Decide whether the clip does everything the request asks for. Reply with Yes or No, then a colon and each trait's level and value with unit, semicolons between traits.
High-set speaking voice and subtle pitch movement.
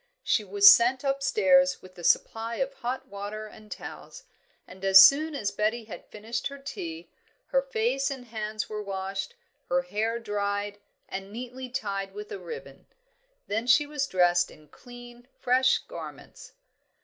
No: high, 225 Hz; average, 5.0 semitones